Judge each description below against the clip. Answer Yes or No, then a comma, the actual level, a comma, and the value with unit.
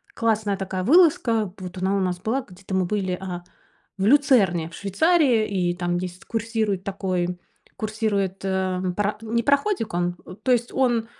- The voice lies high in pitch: Yes, high, 200 Hz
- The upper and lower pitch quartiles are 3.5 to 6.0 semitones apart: Yes, average, 3.8 semitones